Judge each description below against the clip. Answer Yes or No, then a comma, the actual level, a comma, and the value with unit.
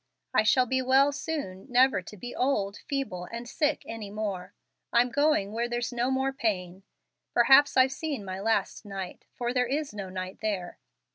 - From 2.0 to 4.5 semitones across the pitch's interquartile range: No, average, 5.1 semitones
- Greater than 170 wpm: Yes, average, 180 wpm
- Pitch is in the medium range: No, high, 240 Hz